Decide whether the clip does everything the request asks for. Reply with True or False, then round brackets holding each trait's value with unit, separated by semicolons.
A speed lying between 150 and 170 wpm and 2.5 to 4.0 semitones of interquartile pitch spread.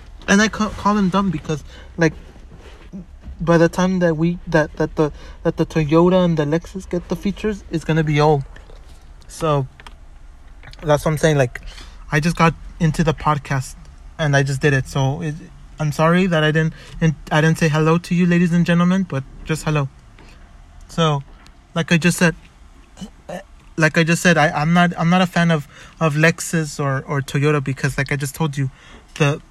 False (190 wpm; 3.6 semitones)